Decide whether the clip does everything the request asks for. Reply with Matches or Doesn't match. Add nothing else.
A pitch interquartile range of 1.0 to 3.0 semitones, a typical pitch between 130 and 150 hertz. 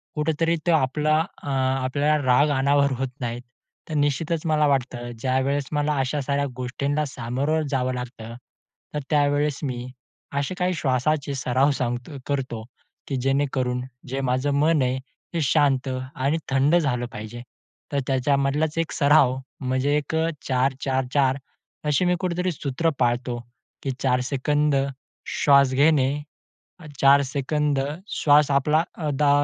Matches